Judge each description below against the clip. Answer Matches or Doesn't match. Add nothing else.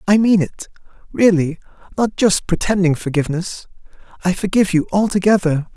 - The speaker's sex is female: Doesn't match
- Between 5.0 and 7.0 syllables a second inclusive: Matches